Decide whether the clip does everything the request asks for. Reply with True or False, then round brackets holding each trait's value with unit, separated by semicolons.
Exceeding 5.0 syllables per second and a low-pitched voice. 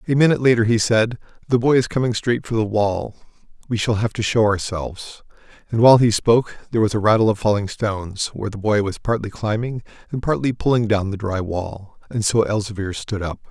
True (5.9 syllables/s; 110 Hz)